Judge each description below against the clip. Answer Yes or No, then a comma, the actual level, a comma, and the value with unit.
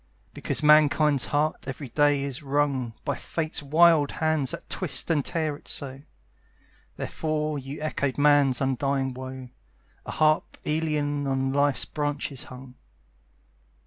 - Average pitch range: No, narrow, 2.3 semitones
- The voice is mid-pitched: Yes, medium, 145 Hz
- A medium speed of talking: No, slow, 130 wpm